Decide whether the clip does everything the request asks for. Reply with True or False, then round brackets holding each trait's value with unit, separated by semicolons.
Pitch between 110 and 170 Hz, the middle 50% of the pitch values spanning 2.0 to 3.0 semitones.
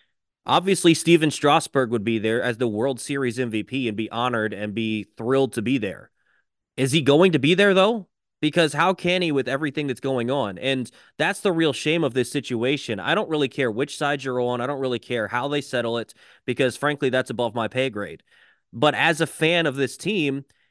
False (135 Hz; 4.0 semitones)